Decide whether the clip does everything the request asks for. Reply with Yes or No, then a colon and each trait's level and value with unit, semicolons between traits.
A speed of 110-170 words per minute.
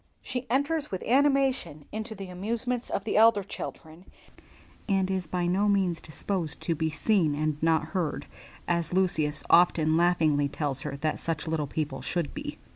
Yes: average, 165 wpm